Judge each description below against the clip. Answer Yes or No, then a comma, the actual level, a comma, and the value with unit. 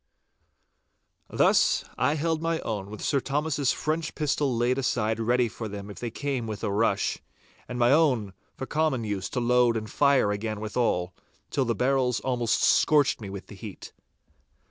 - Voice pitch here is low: Yes, low, 120 Hz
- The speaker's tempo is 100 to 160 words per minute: No, average, 170 wpm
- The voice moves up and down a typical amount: Yes, average, 4.5 semitones